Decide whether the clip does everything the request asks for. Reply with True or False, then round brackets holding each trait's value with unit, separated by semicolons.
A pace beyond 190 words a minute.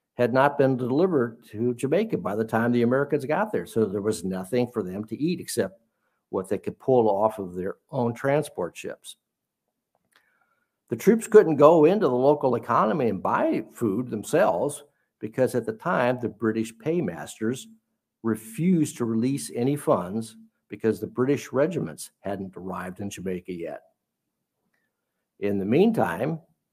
False (155 wpm)